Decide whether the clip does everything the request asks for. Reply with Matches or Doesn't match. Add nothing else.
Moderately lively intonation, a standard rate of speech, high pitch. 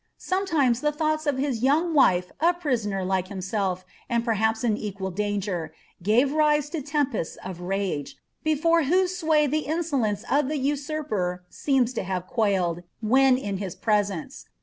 Doesn't match